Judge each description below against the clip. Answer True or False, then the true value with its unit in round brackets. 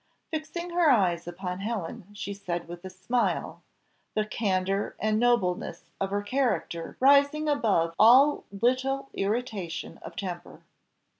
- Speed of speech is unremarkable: False (130 wpm)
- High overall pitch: True (205 Hz)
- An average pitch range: False (5.9 semitones)